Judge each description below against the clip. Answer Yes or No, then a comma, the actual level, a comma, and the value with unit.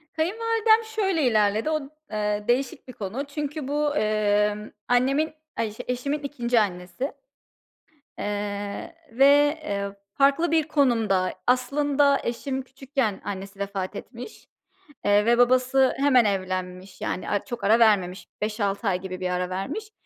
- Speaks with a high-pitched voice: Yes, high, 240 Hz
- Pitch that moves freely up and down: Yes, wide, 5.8 semitones